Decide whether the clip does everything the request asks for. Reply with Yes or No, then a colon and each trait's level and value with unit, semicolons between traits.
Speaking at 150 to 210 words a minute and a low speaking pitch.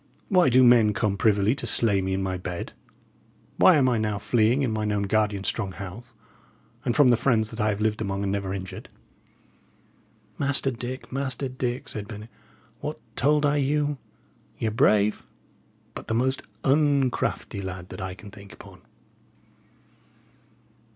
Yes: average, 165 wpm; low, 110 Hz